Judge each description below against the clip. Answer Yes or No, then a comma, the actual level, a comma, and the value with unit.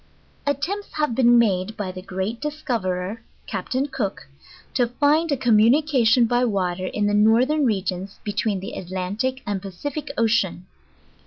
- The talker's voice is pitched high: Yes, high, 225 Hz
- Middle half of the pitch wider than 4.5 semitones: Yes, wide, 5.4 semitones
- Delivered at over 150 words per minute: No, average, 145 wpm